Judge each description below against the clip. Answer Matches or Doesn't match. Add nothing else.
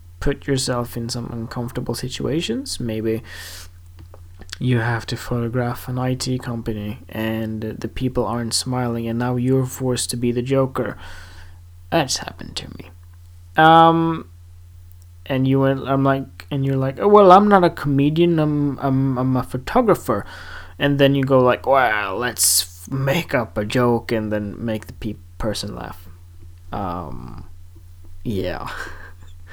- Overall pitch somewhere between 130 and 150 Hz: Doesn't match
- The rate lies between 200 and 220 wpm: Doesn't match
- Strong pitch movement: Matches